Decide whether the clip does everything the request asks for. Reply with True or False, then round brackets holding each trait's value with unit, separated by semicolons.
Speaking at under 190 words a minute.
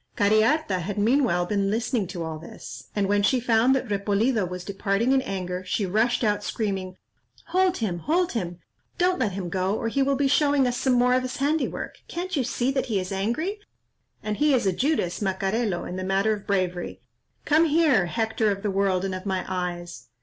False (200 wpm)